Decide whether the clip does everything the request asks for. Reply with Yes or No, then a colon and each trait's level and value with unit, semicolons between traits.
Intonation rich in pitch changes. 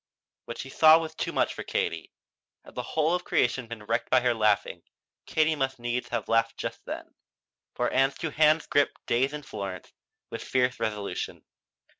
No: average, 4.8 semitones